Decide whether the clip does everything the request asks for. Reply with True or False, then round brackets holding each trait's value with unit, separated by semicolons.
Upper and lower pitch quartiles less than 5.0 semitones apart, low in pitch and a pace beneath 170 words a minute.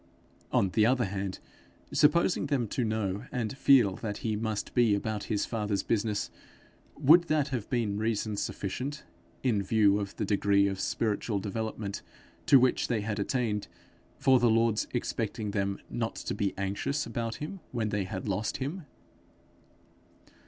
True (3.5 semitones; 110 Hz; 155 wpm)